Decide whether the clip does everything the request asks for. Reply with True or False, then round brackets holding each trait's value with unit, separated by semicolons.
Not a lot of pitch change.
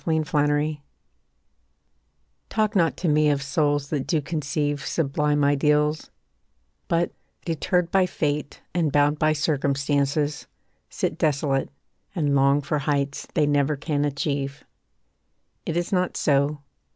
True (1.6 semitones)